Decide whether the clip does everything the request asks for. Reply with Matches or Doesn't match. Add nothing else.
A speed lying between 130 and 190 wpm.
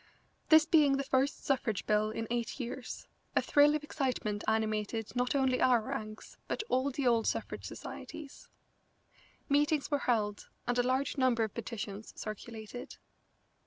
Matches